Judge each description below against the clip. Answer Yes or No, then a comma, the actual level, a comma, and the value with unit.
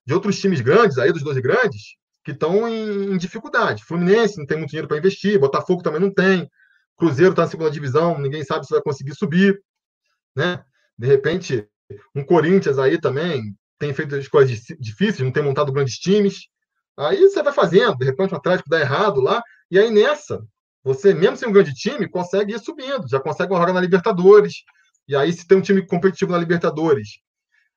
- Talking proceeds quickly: Yes, fast, 195 wpm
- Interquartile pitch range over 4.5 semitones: Yes, average, 5.1 semitones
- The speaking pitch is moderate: Yes, medium, 180 Hz